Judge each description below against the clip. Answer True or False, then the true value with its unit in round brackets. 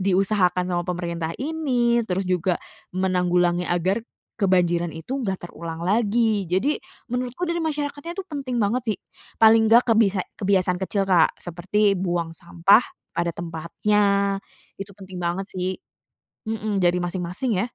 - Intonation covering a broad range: False (4.1 semitones)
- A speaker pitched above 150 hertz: True (190 Hz)